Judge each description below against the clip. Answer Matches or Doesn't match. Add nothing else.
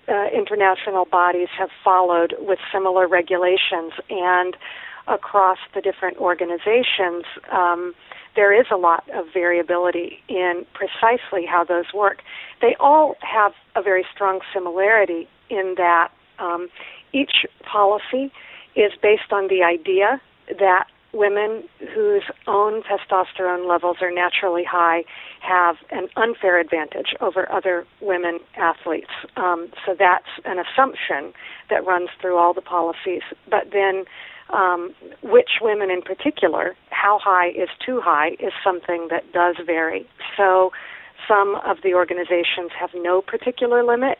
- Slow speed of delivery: Matches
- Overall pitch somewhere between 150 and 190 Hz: Matches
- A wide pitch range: Doesn't match